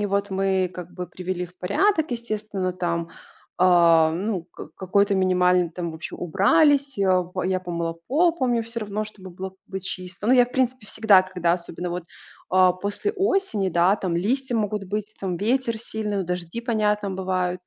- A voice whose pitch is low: No, high, 190 Hz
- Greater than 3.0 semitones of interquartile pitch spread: Yes, average, 3.4 semitones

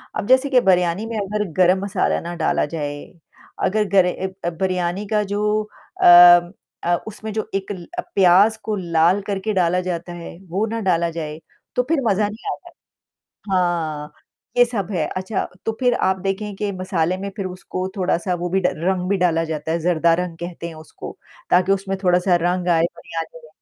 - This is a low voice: No, medium, 185 Hz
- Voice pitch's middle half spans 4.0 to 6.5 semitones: No, average, 2.8 semitones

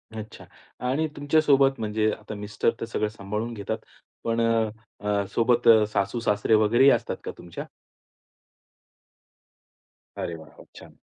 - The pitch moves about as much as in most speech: No, narrow, 2.3 semitones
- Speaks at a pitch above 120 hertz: No, low, 110 Hz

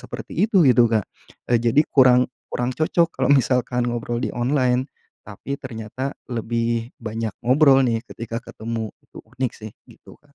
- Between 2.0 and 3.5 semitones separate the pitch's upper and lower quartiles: Yes, narrow, 2.5 semitones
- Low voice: Yes, low, 120 Hz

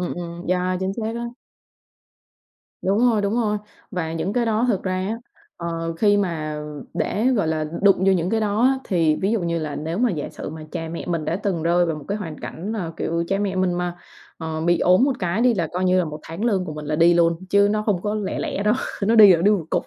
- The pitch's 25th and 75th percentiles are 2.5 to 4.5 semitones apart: Yes, average, 3.8 semitones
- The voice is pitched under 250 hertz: Yes, medium, 185 Hz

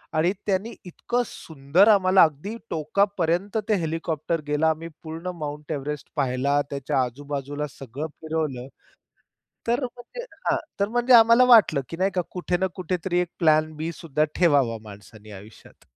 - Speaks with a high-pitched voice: No, medium, 160 Hz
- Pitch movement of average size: Yes, average, 4.6 semitones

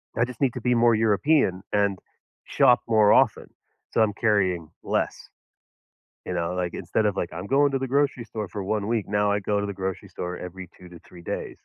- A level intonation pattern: No, average, 4.0 semitones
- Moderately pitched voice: No, low, 105 Hz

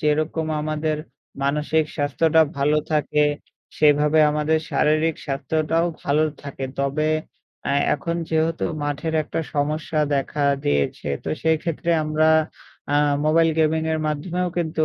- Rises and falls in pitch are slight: Yes, narrow, 1.4 semitones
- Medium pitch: Yes, medium, 155 Hz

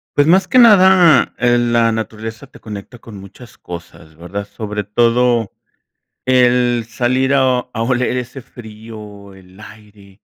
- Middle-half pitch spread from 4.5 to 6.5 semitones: No, average, 3.2 semitones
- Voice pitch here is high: No, low, 115 Hz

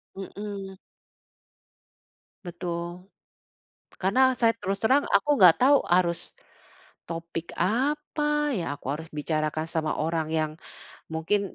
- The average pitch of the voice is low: No, medium, 185 Hz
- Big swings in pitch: Yes, wide, 5.7 semitones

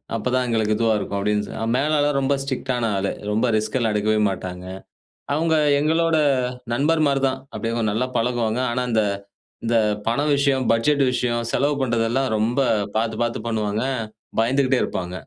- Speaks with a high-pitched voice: No, low, 120 Hz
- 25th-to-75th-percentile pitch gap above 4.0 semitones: No, average, 3.7 semitones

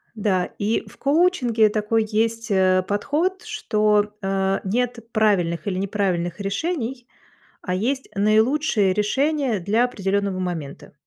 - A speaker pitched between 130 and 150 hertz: No, high, 210 Hz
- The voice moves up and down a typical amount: Yes, average, 4.2 semitones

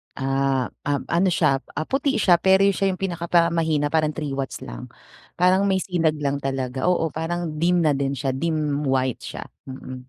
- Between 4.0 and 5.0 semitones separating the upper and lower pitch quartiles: Yes, average, 4.3 semitones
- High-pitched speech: No, medium, 155 Hz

